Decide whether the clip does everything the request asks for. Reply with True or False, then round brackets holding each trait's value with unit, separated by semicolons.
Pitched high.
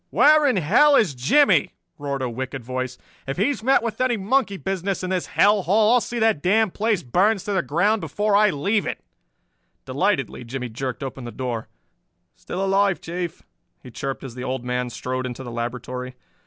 False (175 Hz)